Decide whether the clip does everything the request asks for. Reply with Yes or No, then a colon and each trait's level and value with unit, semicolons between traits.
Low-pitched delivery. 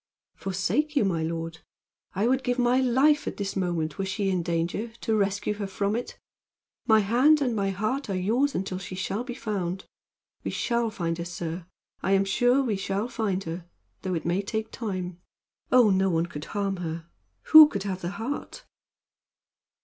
No: high, 195 Hz